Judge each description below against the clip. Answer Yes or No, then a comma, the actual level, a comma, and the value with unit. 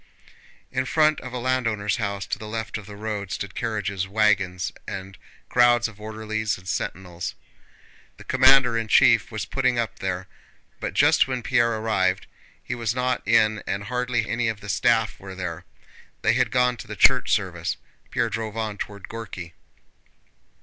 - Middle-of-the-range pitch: No, low, 110 Hz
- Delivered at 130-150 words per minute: No, average, 165 wpm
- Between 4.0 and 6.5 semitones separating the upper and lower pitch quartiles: No, average, 3.3 semitones